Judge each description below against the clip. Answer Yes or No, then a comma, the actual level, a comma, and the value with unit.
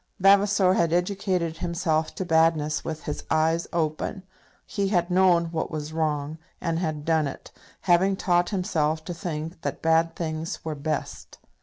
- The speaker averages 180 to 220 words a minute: No, average, 155 wpm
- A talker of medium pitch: Yes, medium, 165 Hz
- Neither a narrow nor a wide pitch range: No, narrow, 2.2 semitones